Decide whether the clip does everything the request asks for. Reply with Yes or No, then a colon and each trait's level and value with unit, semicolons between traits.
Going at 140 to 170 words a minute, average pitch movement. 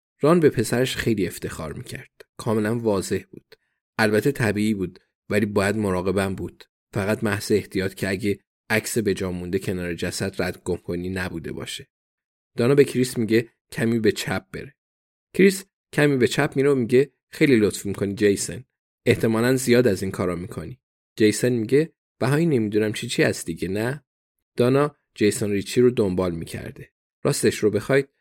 Yes: fast, 155 wpm; average, 4.4 semitones